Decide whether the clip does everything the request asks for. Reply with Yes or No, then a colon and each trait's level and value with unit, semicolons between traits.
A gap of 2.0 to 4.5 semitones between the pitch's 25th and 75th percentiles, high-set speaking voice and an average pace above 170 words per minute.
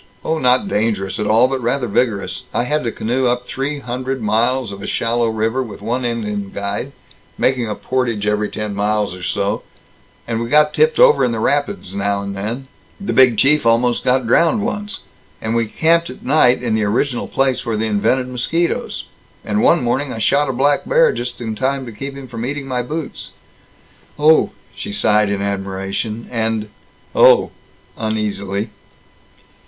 No: average, 3.9 semitones; low, 120 Hz; average, 180 wpm